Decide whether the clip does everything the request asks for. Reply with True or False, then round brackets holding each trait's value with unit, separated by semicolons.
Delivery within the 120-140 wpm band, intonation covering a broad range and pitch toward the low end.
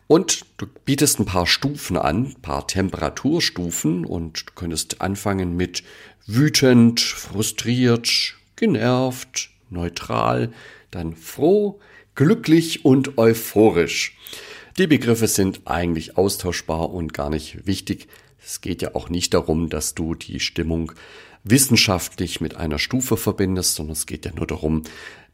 True (130 wpm; 5.9 semitones; 95 Hz)